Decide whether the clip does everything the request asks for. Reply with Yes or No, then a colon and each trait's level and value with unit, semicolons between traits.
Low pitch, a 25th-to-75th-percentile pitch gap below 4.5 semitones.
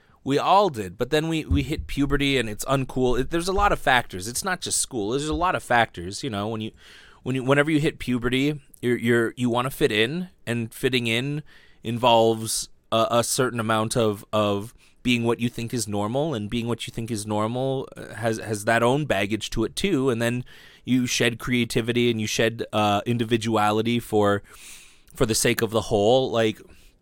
Yes: low, 120 Hz; average, 2.8 semitones